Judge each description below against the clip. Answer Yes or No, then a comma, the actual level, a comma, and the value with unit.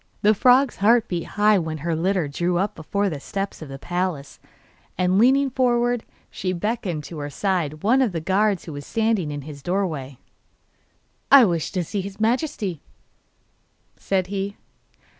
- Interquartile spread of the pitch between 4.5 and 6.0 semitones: Yes, average, 4.9 semitones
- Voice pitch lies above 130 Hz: Yes, high, 190 Hz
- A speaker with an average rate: Yes, average, 165 wpm